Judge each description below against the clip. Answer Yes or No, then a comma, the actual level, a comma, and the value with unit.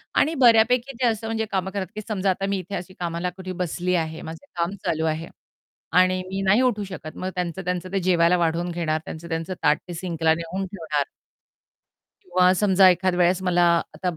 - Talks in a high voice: No, medium, 180 Hz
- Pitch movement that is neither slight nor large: No, narrow, 2.3 semitones